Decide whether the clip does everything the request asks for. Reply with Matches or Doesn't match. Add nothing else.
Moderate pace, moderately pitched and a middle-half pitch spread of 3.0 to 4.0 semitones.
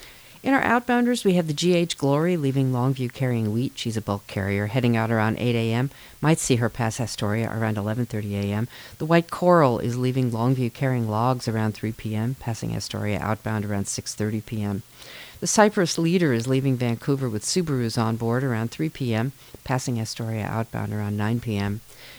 Doesn't match